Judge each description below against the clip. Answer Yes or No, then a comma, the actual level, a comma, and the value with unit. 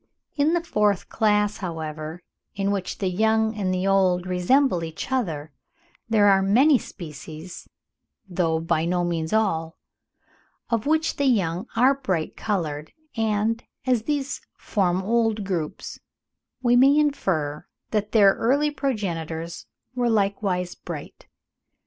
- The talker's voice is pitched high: Yes, high, 200 Hz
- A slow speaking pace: Yes, slow, 130 wpm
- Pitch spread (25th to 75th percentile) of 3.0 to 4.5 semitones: No, average, 5.0 semitones